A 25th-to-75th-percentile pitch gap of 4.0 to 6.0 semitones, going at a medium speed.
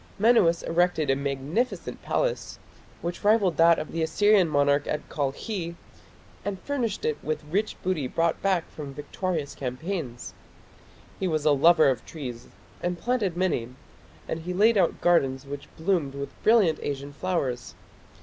Yes: average, 4.7 semitones; average, 150 wpm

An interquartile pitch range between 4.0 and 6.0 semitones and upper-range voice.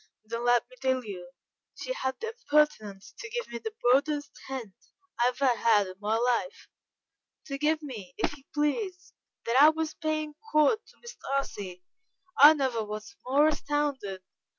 Yes: average, 5.0 semitones; very high, 275 Hz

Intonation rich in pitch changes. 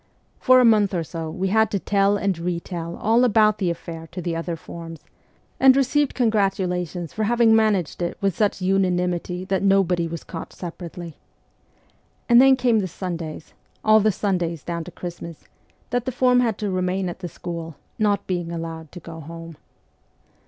No: average, 4.1 semitones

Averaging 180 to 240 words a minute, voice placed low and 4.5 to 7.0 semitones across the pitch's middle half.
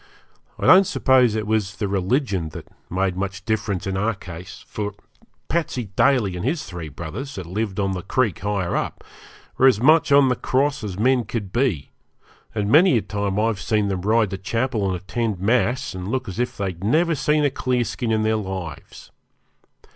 Yes: average, 190 wpm; low, 105 Hz; average, 4.8 semitones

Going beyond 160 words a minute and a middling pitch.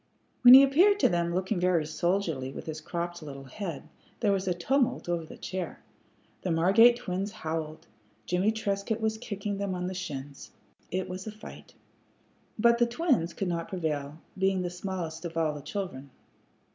Yes: average, 175 wpm; medium, 180 Hz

